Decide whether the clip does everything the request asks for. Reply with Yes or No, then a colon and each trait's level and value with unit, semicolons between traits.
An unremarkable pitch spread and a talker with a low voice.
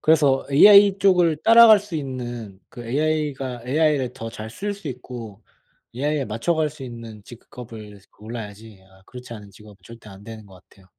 No: wide, 5.9 semitones; low, 125 Hz